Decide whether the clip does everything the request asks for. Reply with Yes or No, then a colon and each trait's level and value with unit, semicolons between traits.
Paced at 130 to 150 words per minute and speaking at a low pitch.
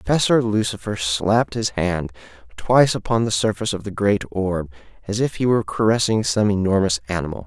No: average, 170 wpm; low, 100 Hz